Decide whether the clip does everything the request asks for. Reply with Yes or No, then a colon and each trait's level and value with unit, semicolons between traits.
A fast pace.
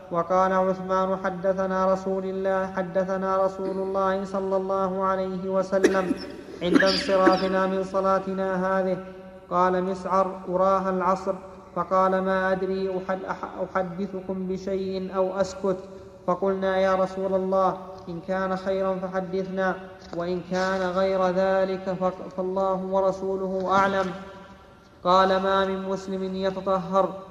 No: average, 110 wpm